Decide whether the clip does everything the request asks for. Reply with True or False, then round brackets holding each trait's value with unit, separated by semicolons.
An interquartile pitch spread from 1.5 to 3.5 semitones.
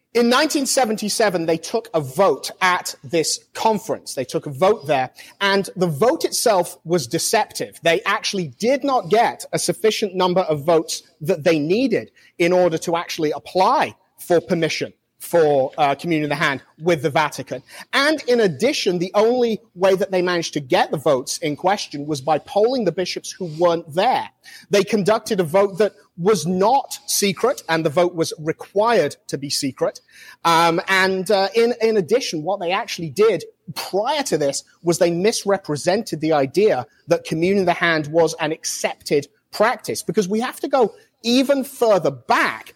False (4.9 semitones)